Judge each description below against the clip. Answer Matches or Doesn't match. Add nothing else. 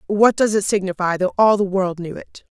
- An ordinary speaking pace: Doesn't match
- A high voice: Matches